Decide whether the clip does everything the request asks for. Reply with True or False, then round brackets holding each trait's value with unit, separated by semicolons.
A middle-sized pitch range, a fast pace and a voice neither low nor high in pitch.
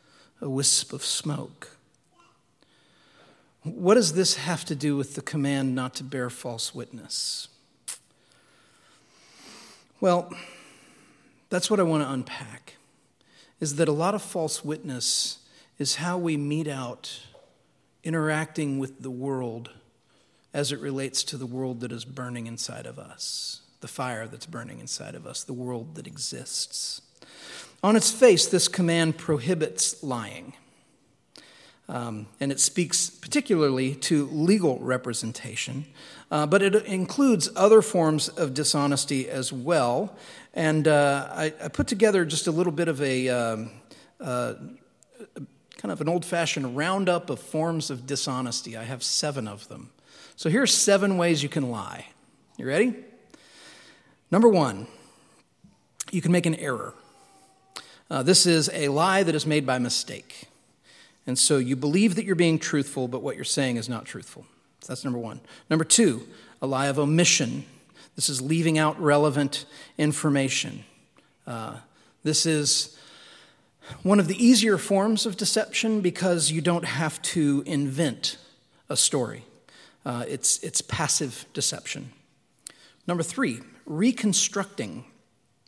False (4.8 semitones; 140 wpm; 155 Hz)